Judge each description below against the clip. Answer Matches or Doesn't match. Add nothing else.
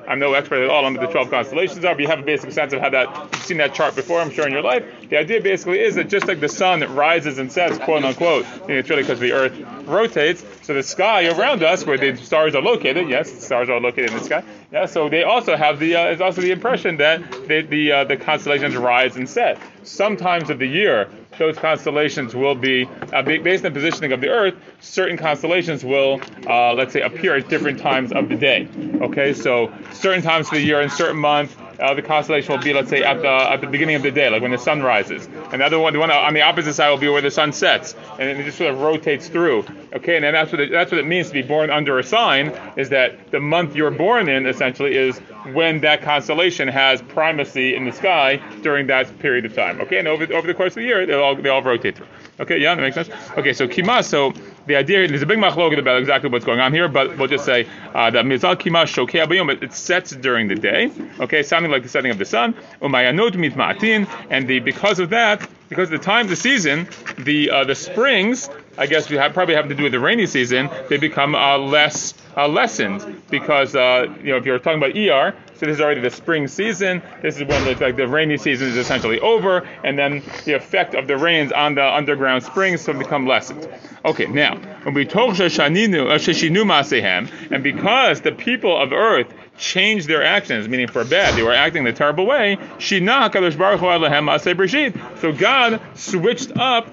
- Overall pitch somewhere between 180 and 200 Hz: Doesn't match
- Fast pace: Matches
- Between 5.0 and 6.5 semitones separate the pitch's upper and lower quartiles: Doesn't match